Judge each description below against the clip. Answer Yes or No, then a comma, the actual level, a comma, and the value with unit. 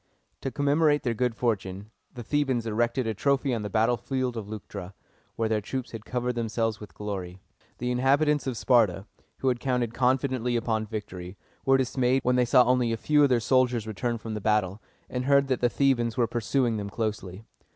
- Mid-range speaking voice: No, low, 120 Hz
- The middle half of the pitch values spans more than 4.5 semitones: No, average, 3.0 semitones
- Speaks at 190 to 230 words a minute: Yes, average, 195 wpm